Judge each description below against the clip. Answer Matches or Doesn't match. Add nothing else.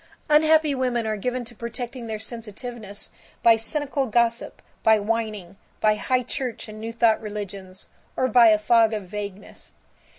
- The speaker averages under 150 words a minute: Doesn't match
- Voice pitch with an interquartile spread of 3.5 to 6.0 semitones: Doesn't match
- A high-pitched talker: Matches